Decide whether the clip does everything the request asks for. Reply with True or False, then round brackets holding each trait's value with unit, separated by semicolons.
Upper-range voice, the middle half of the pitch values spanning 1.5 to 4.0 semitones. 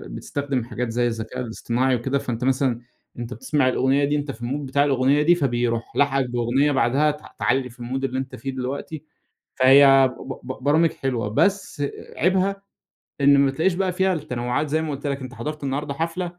False (135 Hz; 2.8 semitones)